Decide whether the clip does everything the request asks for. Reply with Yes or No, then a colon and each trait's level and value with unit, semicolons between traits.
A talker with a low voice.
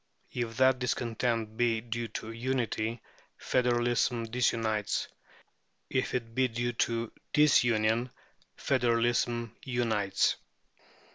Yes: low, 120 Hz